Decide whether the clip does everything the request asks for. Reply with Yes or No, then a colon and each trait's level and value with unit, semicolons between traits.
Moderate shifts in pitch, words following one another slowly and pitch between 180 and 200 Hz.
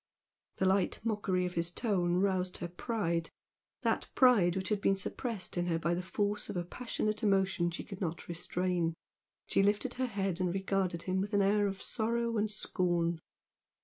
No: average, 3.0 semitones; average, 180 wpm; high, 190 Hz